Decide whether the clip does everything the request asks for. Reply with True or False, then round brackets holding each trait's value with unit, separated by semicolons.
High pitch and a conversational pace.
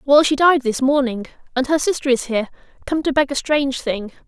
False (270 Hz; 210 wpm)